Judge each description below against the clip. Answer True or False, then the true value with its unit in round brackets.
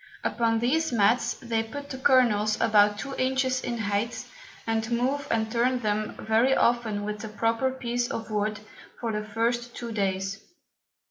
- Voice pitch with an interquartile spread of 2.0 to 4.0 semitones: True (2.5 semitones)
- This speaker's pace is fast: False (160 wpm)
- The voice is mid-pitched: False (230 Hz)